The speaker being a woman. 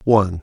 No: male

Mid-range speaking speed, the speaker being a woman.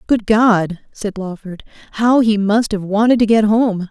Yes: average, 185 wpm; female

